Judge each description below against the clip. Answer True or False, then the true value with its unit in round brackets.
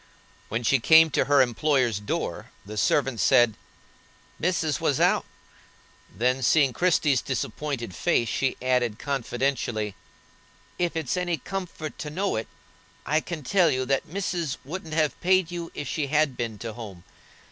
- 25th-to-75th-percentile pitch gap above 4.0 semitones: True (5.0 semitones)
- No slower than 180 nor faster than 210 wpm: False (155 wpm)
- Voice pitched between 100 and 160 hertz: True (140 Hz)